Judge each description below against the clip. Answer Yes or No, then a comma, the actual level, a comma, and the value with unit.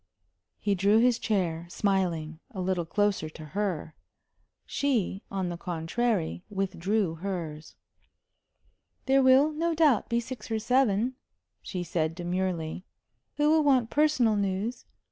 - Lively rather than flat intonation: Yes, wide, 5.7 semitones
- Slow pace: Yes, slow, 125 wpm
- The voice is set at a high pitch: Yes, high, 200 Hz